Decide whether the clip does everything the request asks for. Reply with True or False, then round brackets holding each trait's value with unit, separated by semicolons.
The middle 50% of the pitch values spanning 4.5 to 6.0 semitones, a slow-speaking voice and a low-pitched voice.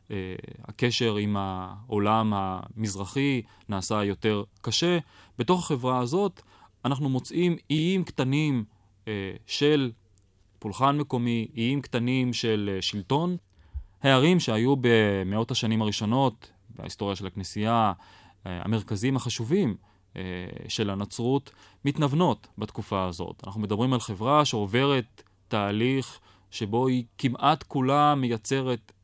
True (5.0 semitones; 95 wpm; 115 Hz)